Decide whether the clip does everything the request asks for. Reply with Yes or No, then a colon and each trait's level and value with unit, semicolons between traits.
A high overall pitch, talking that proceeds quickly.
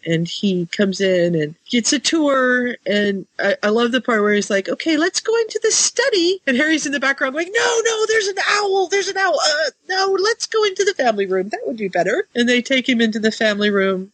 Yes: very high, 260 Hz; fast, 240 wpm